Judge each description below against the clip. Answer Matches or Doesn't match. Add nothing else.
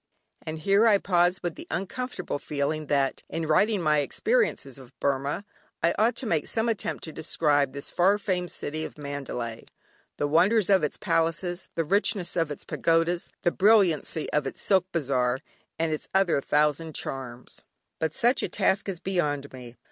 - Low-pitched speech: Doesn't match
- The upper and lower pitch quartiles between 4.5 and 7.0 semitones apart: Matches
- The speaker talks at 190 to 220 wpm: Doesn't match